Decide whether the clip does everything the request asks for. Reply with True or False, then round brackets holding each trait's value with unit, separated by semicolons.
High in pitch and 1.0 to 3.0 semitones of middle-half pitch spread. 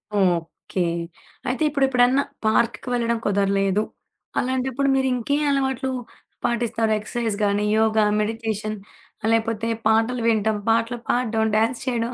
True (230 Hz; 2.6 semitones)